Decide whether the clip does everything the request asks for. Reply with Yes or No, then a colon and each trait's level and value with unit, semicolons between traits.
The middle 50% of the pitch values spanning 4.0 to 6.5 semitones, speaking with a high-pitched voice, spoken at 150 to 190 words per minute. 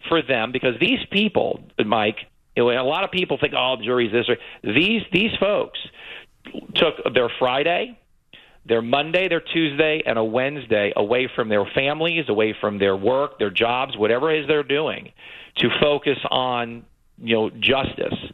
No: average, 5.0 semitones; low, 135 Hz; average, 160 wpm